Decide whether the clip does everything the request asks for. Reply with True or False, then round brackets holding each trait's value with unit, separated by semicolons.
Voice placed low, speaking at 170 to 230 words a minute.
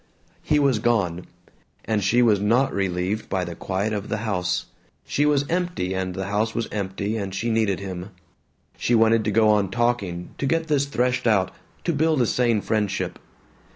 True (110 Hz; 185 wpm)